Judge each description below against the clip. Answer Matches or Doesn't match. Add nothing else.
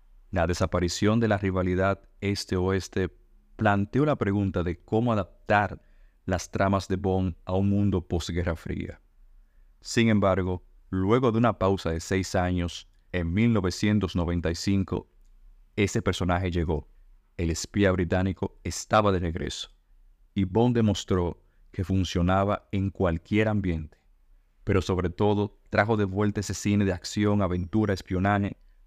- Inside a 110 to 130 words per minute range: Matches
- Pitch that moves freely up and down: Doesn't match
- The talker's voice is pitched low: Matches